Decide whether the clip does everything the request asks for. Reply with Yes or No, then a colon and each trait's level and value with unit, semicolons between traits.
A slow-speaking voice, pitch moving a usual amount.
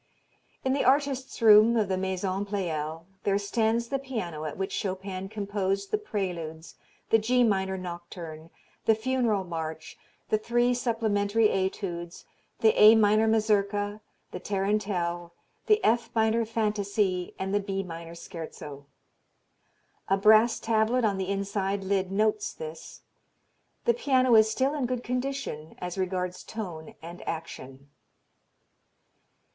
Yes: slow, 130 wpm; average, 3.6 semitones